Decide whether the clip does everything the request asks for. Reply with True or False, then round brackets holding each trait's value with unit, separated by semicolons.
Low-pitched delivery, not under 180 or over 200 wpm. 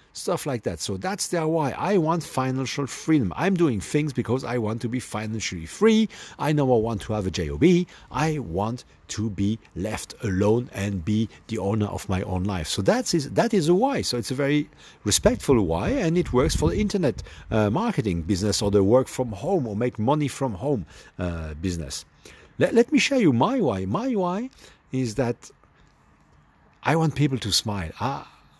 True (125 Hz; 195 wpm)